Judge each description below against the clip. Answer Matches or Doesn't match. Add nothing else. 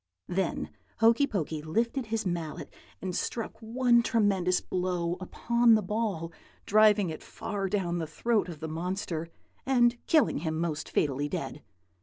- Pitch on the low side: Doesn't match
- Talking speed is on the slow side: Doesn't match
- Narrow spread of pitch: Doesn't match